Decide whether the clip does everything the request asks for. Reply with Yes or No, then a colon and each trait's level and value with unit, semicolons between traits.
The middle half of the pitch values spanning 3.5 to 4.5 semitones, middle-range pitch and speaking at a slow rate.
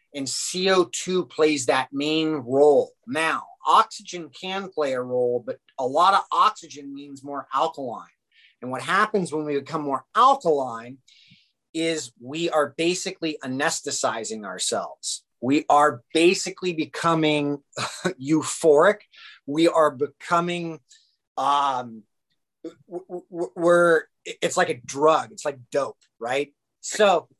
Yes: average, 3.8 semitones; medium, 155 Hz; slow, 120 wpm